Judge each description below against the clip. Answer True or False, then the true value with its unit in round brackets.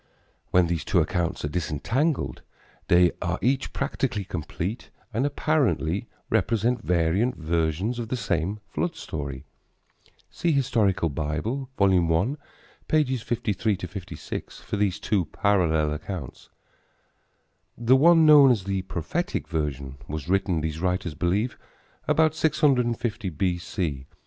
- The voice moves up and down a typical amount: False (6.8 semitones)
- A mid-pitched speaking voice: False (95 Hz)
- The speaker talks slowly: True (115 wpm)